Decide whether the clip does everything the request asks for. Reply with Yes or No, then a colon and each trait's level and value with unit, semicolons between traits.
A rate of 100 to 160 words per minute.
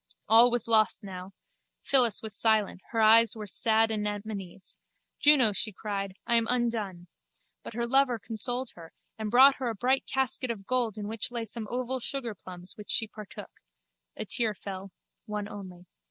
No: average, 170 wpm